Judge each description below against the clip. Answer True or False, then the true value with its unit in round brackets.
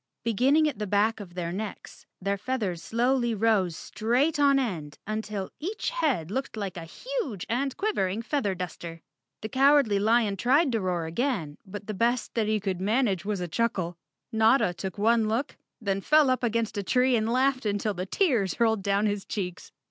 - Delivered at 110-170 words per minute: False (185 wpm)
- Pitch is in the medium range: False (215 Hz)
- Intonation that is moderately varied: True (4.8 semitones)